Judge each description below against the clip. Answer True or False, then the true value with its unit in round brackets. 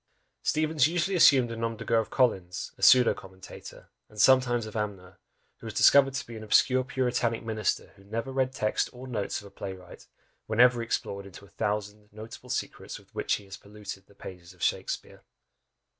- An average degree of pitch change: True (4.1 semitones)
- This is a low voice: True (115 Hz)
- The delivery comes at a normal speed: True (195 wpm)